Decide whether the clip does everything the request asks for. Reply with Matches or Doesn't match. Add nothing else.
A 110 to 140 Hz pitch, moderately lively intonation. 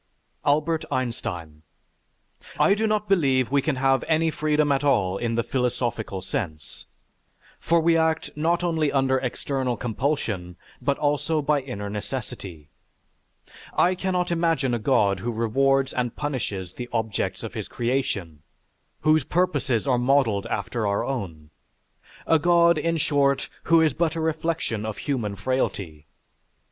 Doesn't match